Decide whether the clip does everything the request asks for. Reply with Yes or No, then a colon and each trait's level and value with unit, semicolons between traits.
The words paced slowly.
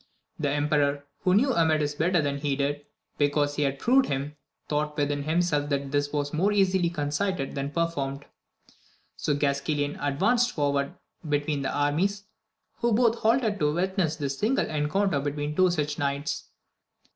No: average, 155 wpm